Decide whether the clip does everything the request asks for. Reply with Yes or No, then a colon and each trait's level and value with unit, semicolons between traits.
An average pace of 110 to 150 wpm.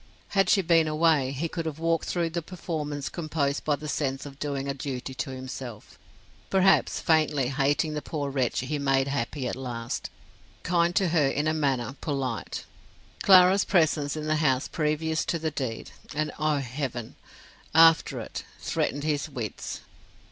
No: average, 165 wpm